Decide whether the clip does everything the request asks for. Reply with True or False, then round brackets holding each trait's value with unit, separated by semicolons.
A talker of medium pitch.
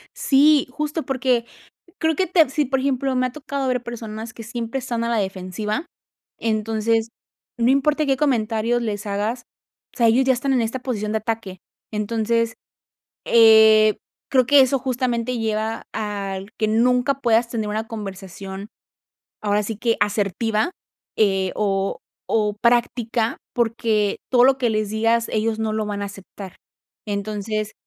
False (225 Hz)